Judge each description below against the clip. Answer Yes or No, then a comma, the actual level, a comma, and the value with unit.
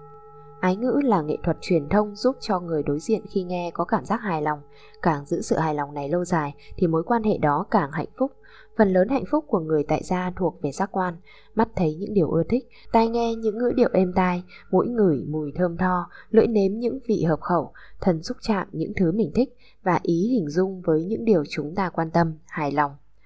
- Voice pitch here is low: No, medium, 185 Hz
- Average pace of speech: Yes, average, 235 wpm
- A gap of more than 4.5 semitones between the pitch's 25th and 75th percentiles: Yes, wide, 5.4 semitones